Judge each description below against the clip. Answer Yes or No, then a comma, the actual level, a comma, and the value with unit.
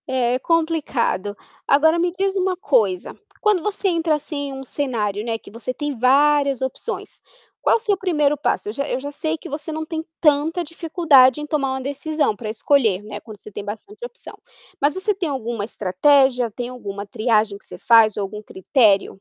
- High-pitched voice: Yes, very high, 275 Hz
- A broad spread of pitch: Yes, wide, 6.0 semitones